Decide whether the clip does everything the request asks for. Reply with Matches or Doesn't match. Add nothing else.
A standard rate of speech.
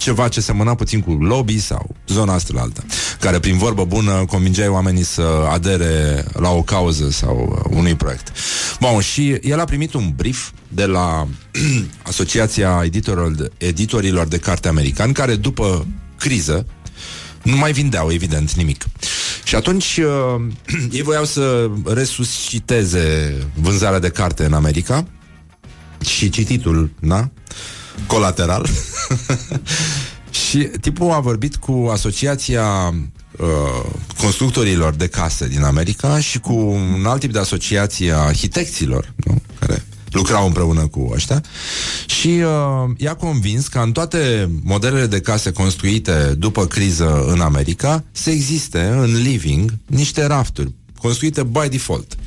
Matches